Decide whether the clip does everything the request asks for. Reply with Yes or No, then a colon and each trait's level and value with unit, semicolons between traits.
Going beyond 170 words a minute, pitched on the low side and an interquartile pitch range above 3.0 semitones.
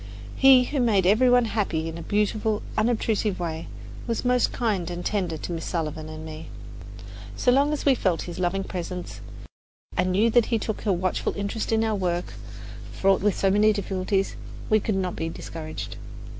No: average, 185 wpm; high, 195 Hz; average, 4.1 semitones